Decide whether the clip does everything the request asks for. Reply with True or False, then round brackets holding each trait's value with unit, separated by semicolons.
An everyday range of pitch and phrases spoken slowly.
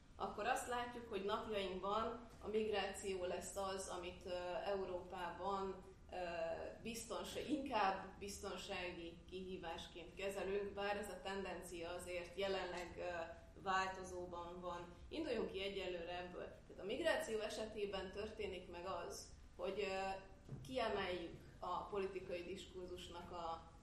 False (2.1 semitones; 100 wpm)